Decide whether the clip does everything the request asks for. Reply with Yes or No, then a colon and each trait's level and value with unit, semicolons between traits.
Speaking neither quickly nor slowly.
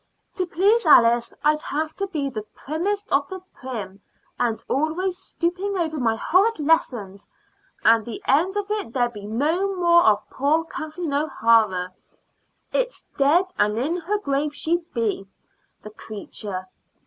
Yes: average, 150 wpm